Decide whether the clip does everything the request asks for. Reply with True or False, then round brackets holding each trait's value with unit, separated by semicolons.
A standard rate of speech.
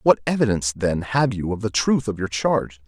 False (230 wpm)